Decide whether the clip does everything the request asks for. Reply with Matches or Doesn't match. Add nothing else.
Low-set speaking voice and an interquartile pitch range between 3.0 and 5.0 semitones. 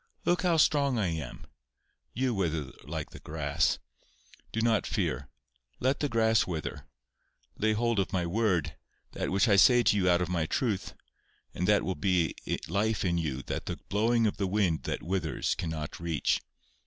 Doesn't match